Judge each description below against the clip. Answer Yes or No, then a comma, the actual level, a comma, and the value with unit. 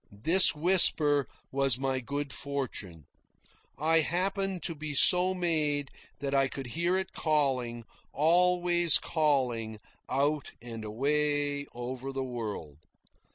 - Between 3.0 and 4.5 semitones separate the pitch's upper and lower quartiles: Yes, average, 4.2 semitones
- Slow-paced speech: Yes, slow, 115 wpm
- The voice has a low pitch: No, medium, 145 Hz